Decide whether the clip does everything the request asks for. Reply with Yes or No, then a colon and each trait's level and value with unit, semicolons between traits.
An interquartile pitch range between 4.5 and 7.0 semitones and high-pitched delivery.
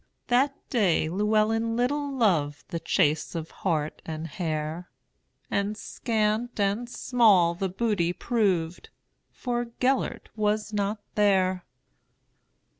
Yes: average, 5.2 semitones; high, 205 Hz